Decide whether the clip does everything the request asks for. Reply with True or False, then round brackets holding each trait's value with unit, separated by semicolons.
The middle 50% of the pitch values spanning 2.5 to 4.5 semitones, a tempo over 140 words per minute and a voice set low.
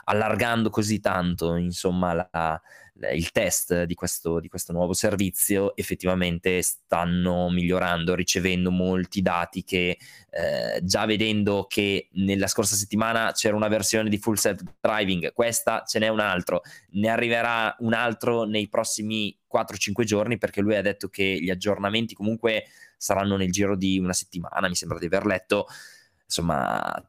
True (3.0 semitones; 150 wpm; 100 Hz)